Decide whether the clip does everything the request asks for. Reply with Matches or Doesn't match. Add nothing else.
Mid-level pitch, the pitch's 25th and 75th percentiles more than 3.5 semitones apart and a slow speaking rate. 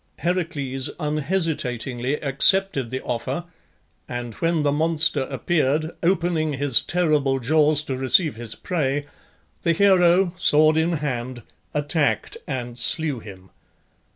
Matches